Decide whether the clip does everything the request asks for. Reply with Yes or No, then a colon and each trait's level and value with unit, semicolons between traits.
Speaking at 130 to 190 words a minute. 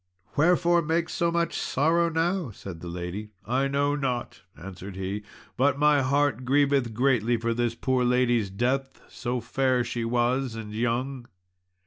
Yes: average, 150 wpm